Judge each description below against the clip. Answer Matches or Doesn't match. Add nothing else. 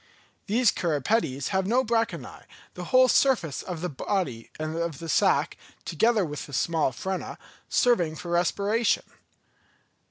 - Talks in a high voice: Doesn't match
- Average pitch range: Doesn't match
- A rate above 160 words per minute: Doesn't match